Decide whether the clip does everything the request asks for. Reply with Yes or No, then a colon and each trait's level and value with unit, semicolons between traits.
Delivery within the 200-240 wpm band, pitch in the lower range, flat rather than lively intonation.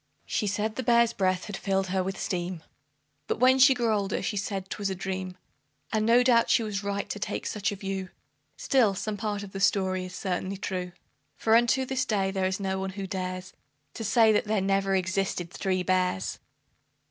No: fast, 205 wpm; high, 195 Hz; narrow, 2.3 semitones